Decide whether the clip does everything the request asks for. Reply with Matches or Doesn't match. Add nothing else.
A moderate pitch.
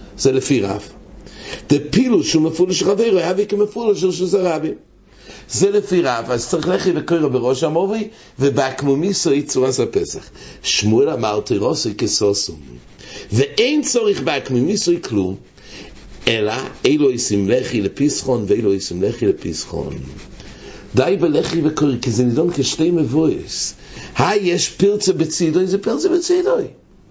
Matches